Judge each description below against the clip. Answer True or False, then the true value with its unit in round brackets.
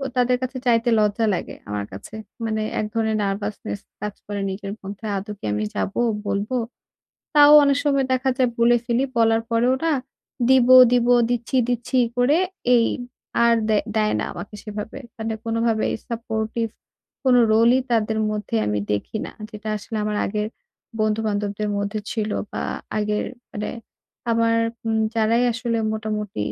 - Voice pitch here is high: True (220 Hz)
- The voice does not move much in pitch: True (2.2 semitones)